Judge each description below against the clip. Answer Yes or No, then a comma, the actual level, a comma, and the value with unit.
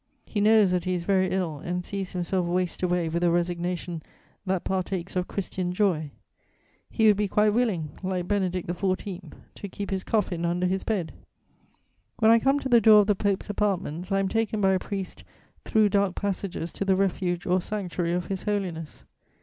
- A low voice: No, medium, 185 Hz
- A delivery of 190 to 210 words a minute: Yes, average, 195 wpm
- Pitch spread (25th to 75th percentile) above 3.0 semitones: No, narrow, 2.4 semitones